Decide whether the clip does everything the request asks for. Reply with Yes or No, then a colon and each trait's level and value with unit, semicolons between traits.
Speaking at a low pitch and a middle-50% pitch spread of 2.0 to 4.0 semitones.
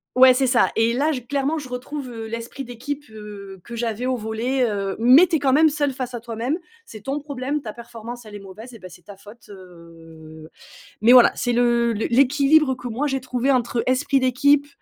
No: high, 245 Hz; average, 3.5 semitones